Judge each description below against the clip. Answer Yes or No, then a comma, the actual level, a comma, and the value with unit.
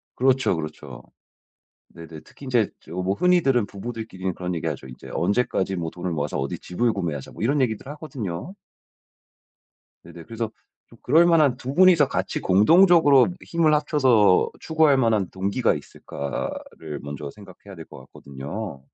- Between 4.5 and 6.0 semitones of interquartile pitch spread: No, wide, 8.0 semitones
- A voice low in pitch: Yes, low, 105 Hz